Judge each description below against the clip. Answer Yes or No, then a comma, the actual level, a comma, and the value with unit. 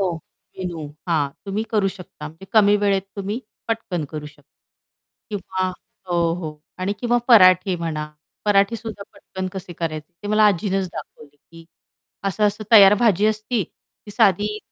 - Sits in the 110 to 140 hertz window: No, high, 195 Hz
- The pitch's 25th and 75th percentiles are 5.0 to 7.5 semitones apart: No, average, 3.3 semitones